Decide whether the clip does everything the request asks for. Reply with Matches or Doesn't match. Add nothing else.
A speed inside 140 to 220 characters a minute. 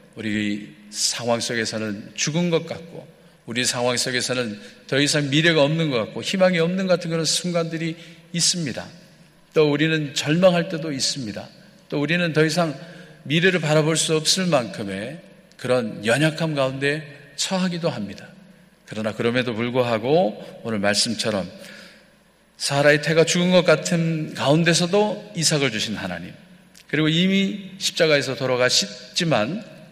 Doesn't match